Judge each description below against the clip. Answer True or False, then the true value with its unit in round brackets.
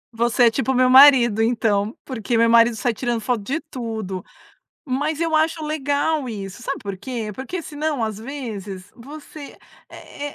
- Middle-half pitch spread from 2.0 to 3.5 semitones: False (4.4 semitones)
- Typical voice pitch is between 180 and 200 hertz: False (245 Hz)